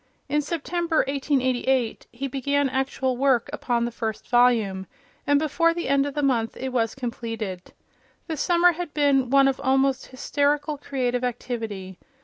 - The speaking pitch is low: No, very high, 265 Hz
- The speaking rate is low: No, average, 150 wpm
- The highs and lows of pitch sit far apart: No, average, 2.9 semitones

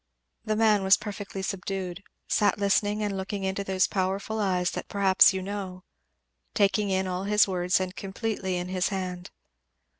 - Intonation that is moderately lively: No, narrow, 1.6 semitones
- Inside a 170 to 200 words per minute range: No, average, 160 wpm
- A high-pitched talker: Yes, high, 195 Hz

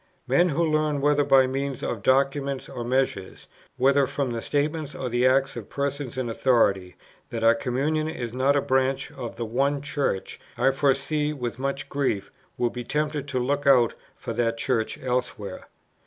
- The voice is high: No, low, 135 Hz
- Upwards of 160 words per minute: Yes, average, 175 wpm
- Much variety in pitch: No, average, 2.8 semitones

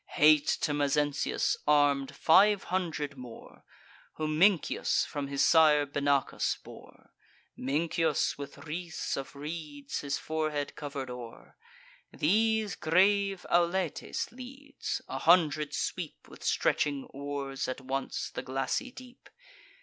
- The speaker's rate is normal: No, slow, 115 wpm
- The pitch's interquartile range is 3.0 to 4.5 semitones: Yes, average, 3.7 semitones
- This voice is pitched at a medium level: Yes, medium, 150 Hz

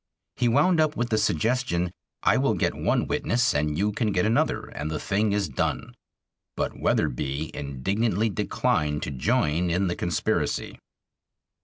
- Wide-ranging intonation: Yes, wide, 7.0 semitones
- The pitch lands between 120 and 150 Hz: No, very low, 95 Hz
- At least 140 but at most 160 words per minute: Yes, average, 155 wpm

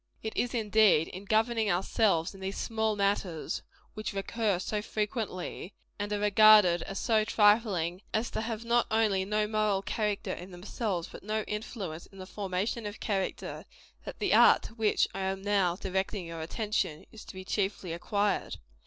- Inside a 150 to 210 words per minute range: Yes, average, 170 wpm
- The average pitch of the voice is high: Yes, high, 205 Hz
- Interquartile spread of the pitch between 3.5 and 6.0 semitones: No, narrow, 2.4 semitones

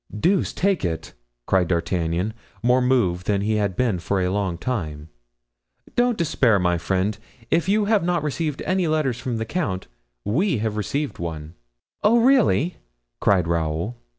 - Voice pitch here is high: No, low, 110 Hz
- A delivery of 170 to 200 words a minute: No, average, 155 wpm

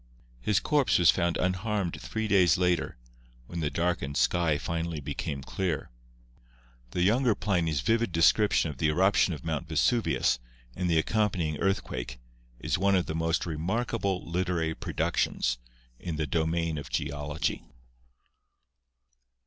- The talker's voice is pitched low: Yes, very low, 85 Hz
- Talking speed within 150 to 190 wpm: No, slow, 135 wpm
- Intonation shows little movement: No, average, 3.5 semitones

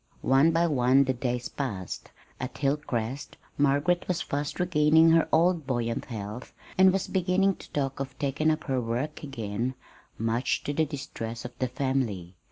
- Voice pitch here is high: No, low, 135 Hz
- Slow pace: No, average, 165 wpm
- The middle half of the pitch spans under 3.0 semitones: No, average, 4.3 semitones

